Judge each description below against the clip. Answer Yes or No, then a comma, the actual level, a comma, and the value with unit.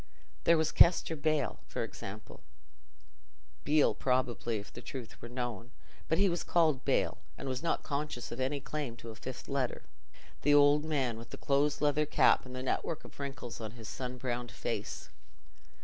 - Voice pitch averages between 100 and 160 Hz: Yes, low, 135 Hz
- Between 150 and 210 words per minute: Yes, average, 180 wpm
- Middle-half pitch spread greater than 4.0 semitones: No, average, 3.6 semitones